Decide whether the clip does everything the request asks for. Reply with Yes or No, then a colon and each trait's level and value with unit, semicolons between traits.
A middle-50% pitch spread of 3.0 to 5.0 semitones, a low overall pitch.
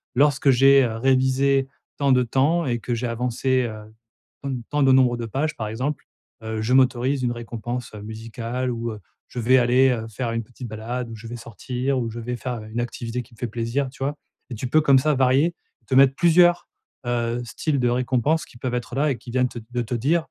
No: narrow, 2.4 semitones; low, 125 Hz